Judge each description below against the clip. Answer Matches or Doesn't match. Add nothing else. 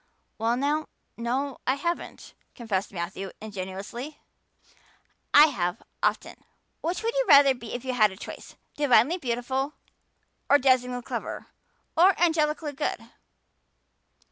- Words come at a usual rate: Doesn't match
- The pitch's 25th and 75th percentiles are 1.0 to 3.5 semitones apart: Doesn't match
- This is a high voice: Matches